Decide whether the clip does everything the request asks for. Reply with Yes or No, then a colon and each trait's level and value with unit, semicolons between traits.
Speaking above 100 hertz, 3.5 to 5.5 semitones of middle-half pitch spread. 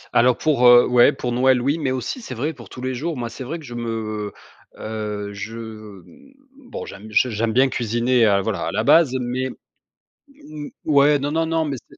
Yes: low, 125 Hz; average, 4.1 semitones